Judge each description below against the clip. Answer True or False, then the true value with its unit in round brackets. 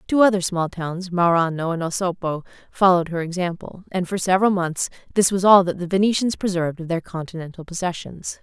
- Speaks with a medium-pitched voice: True (180 Hz)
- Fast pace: False (180 wpm)